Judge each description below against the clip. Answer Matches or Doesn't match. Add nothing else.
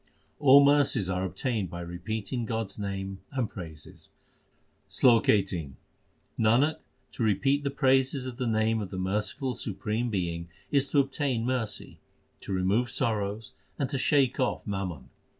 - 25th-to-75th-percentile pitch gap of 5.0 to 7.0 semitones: Matches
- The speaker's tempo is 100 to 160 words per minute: Matches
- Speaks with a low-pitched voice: Matches